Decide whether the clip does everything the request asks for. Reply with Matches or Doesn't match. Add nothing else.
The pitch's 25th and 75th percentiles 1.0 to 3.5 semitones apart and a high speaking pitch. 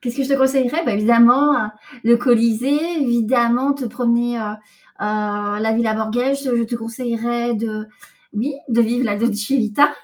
Matches